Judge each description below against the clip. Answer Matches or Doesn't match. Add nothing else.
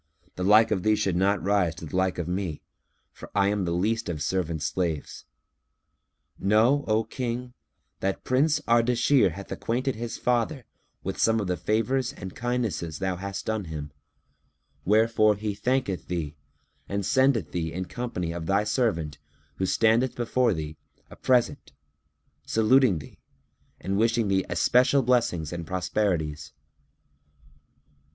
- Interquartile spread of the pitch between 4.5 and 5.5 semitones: Matches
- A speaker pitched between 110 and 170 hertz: Doesn't match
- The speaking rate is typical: Matches